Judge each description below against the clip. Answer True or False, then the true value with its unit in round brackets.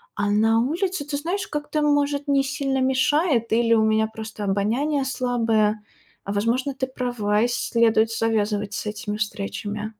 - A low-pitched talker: False (230 Hz)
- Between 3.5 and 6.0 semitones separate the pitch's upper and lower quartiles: True (4.6 semitones)